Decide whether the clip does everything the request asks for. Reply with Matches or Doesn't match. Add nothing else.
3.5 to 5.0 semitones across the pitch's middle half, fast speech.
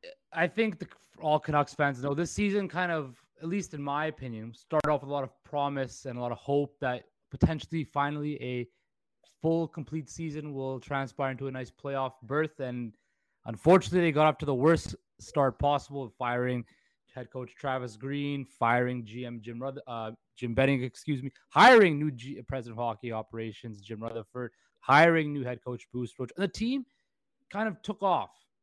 Doesn't match